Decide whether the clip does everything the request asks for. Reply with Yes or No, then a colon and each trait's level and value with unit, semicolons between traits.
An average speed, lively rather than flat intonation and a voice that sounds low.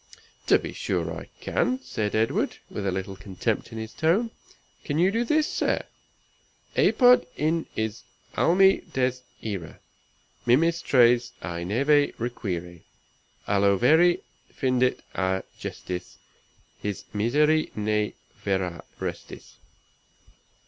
No: slow, 120 wpm; wide, 8.0 semitones; low, 120 Hz